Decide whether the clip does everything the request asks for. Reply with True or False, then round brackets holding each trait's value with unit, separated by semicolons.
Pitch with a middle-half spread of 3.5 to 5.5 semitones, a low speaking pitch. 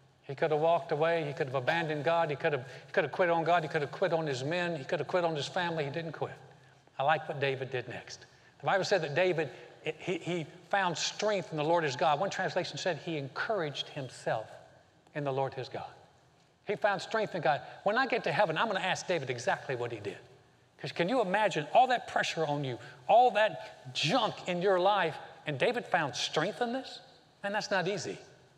False (4.5 semitones; 165 Hz)